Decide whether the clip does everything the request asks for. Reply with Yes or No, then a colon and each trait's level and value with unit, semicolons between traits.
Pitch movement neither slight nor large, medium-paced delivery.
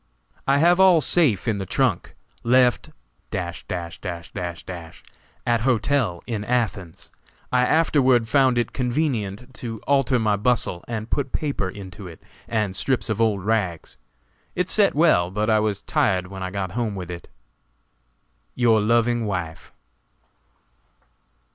No: average, 5.0 semitones; slow, 130 wpm